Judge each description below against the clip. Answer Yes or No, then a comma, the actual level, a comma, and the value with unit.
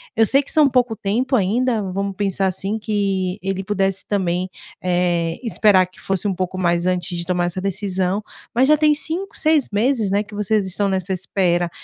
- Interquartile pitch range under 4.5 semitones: Yes, average, 3.0 semitones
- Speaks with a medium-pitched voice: No, high, 195 Hz